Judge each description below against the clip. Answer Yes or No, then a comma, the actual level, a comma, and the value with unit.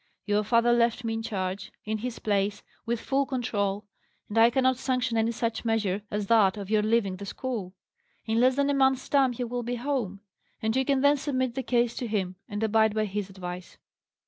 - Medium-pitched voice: No, high, 225 Hz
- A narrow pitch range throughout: No, average, 3.4 semitones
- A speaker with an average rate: No, fast, 210 wpm